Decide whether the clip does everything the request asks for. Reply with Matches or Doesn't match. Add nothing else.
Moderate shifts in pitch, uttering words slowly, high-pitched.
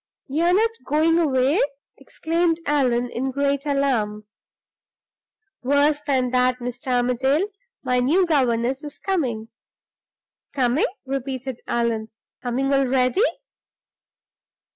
Matches